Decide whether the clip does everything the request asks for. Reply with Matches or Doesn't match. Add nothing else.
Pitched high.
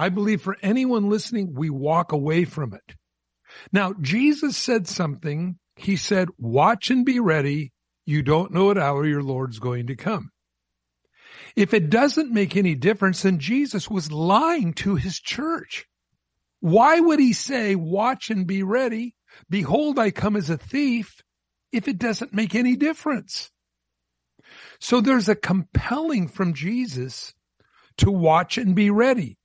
Matches